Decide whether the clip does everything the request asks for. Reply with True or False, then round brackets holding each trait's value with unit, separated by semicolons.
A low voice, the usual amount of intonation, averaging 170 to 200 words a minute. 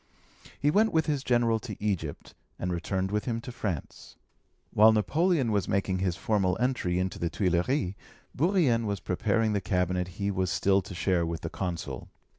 True (100 Hz; 4.6 semitones; 175 wpm)